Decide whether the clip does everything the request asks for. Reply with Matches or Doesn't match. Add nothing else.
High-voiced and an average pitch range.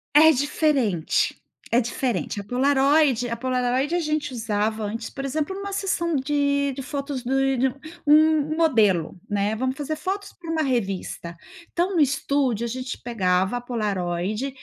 Matches